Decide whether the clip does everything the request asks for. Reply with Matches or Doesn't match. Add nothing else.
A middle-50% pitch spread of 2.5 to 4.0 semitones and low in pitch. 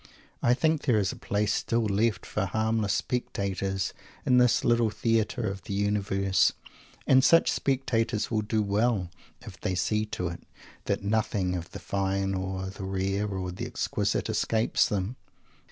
Matches